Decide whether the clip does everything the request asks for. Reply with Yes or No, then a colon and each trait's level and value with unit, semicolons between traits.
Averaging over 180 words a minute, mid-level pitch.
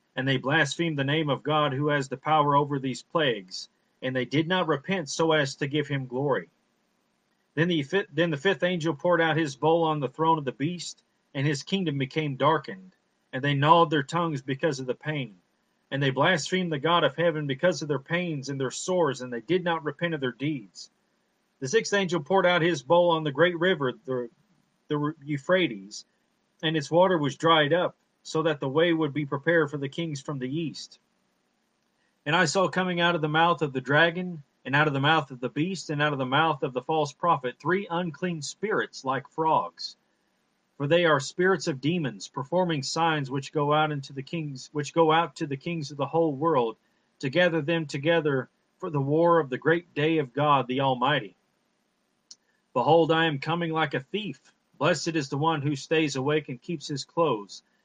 Yes: fast, 205 wpm; medium, 155 Hz